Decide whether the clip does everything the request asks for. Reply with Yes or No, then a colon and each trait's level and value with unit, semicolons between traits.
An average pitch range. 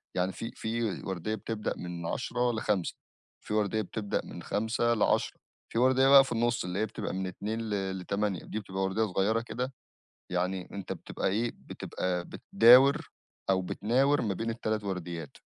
Yes: average, 3.5 semitones